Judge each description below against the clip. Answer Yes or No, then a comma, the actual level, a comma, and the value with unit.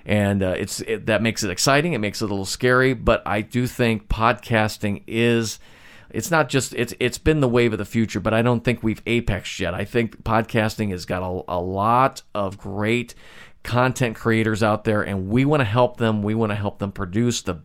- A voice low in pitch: Yes, low, 110 Hz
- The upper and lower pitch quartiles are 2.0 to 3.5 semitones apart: Yes, average, 2.8 semitones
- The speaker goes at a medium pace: No, fast, 220 wpm